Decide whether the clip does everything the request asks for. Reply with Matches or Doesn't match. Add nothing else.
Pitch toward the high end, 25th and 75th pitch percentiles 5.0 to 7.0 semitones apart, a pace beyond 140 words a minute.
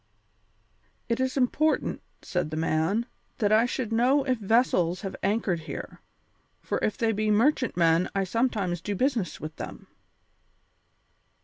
Doesn't match